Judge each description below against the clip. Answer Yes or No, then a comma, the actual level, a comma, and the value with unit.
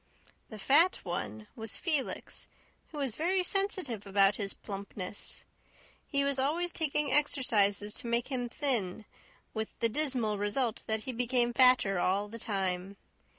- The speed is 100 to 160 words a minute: Yes, average, 145 wpm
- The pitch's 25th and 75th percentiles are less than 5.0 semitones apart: No, wide, 5.5 semitones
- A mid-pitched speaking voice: No, high, 235 Hz